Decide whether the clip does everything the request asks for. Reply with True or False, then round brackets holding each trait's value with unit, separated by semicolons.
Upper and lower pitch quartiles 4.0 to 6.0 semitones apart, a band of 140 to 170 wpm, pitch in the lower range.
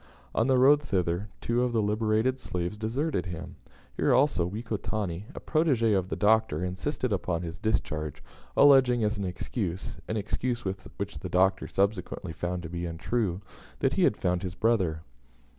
True (4.6 semitones; 165 wpm; 100 Hz)